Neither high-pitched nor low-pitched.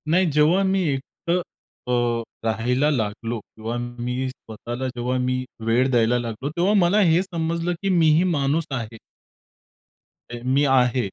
No: low, 130 Hz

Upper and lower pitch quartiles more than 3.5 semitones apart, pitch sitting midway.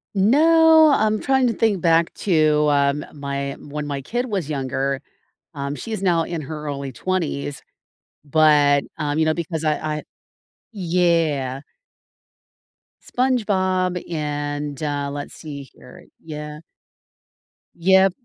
Yes: average, 4.5 semitones; medium, 155 Hz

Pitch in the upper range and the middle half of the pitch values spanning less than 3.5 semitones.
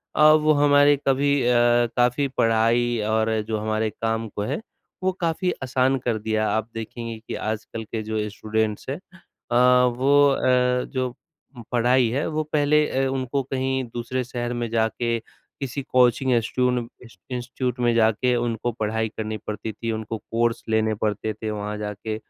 No: low, 120 Hz; average, 2.8 semitones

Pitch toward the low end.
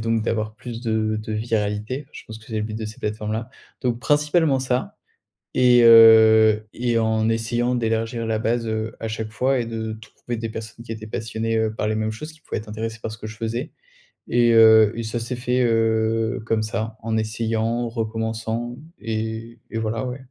Yes: low, 115 Hz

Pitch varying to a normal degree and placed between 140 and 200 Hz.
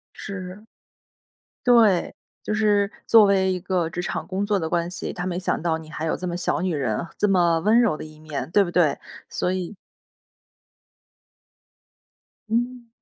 Yes: average, 3.3 semitones; medium, 185 Hz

